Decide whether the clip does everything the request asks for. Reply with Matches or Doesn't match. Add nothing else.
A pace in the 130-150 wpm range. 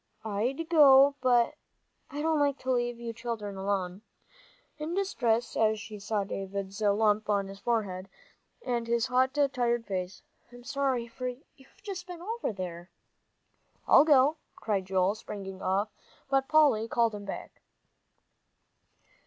Matches